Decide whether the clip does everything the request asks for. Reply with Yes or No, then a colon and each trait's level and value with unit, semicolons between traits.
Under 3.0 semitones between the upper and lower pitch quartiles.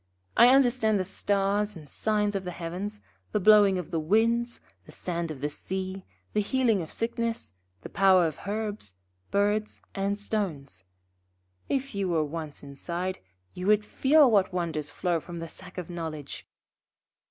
No: average, 4.1 semitones